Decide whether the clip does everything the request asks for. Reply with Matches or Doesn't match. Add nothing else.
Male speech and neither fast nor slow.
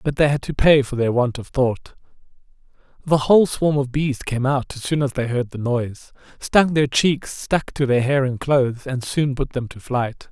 Doesn't match